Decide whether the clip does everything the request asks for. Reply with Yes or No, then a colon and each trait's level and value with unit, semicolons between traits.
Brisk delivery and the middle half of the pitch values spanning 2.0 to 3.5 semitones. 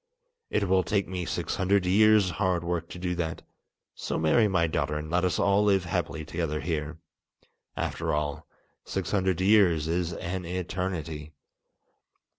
No: average, 155 wpm; average, 2.7 semitones